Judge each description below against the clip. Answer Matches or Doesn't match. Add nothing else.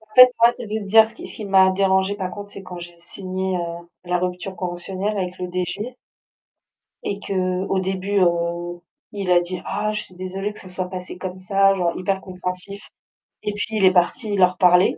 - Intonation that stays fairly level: Matches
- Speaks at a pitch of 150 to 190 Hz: Matches